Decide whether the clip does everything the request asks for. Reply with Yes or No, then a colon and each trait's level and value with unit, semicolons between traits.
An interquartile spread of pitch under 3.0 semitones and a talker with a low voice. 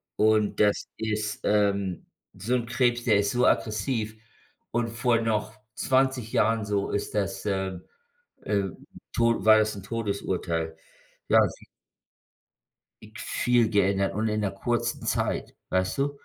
Yes: narrow, 2.6 semitones; low, 110 Hz